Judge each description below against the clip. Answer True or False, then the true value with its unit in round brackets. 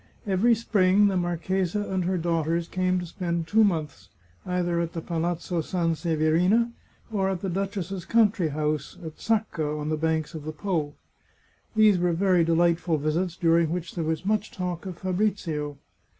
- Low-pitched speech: False (175 Hz)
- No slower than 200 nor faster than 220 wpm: False (165 wpm)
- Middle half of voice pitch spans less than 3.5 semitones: True (2.9 semitones)